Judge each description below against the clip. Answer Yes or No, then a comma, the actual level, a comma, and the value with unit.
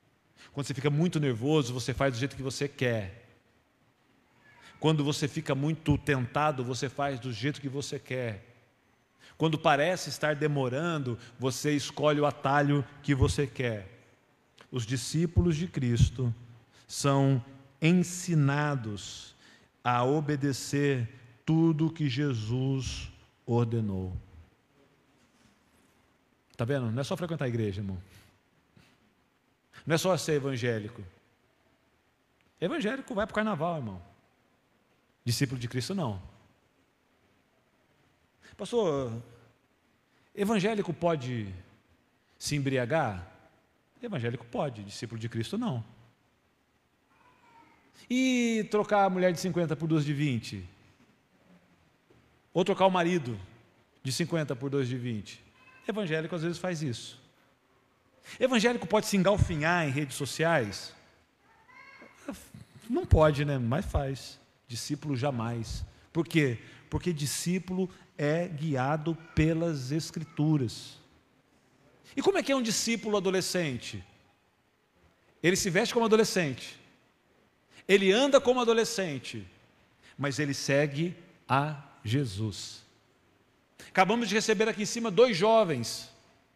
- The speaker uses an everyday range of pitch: No, wide, 5.8 semitones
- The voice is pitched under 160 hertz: Yes, medium, 140 Hz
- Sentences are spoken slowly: Yes, slow, 110 wpm